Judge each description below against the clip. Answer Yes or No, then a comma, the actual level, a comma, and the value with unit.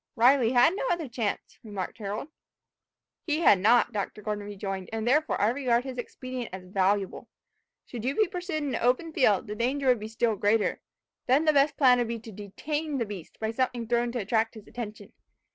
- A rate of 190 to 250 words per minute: Yes, average, 200 wpm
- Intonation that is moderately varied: Yes, average, 4.0 semitones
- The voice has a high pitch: Yes, high, 235 Hz